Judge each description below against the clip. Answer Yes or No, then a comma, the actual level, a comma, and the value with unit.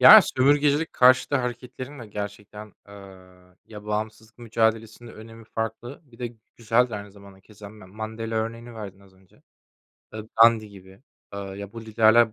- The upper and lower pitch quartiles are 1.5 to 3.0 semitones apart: Yes, narrow, 2.5 semitones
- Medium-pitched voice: No, low, 110 Hz